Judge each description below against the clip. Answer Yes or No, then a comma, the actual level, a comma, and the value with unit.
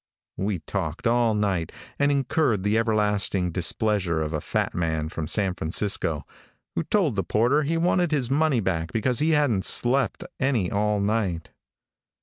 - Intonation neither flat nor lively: No, wide, 6.4 semitones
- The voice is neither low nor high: No, low, 105 Hz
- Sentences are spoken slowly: No, average, 155 wpm